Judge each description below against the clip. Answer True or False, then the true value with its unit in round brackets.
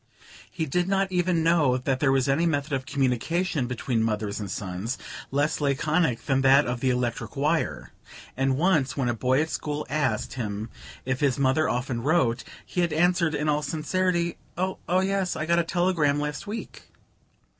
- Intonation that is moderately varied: True (4.9 semitones)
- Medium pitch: True (145 Hz)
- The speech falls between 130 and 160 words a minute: False (175 wpm)